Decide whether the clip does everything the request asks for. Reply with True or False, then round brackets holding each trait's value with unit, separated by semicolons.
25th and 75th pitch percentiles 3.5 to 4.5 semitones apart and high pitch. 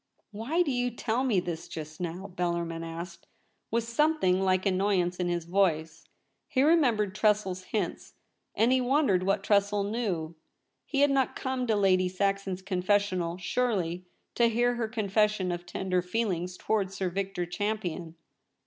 True (4.0 semitones; 195 Hz)